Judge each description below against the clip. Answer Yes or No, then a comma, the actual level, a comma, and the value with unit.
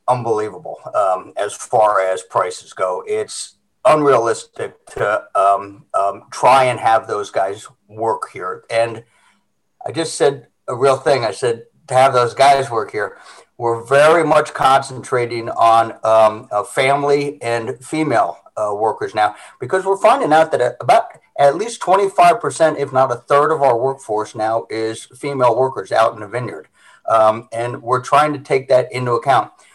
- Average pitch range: No, wide, 5.8 semitones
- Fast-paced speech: No, average, 160 wpm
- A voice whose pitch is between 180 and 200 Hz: No, low, 135 Hz